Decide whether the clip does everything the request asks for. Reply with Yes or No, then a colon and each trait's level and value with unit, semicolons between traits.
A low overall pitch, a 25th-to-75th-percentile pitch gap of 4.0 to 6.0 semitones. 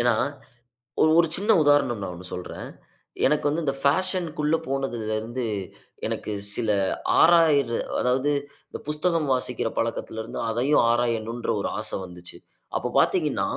Yes: low, 130 Hz; average, 4.8 semitones